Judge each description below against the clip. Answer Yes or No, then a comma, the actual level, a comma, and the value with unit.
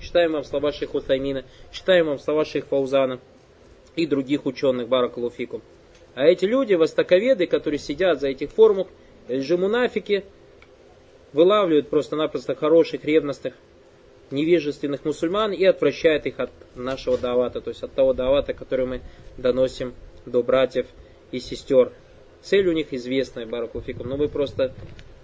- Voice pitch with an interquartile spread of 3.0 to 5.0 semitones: No, wide, 5.4 semitones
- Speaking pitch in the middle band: Yes, medium, 145 Hz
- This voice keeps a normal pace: Yes, average, 135 wpm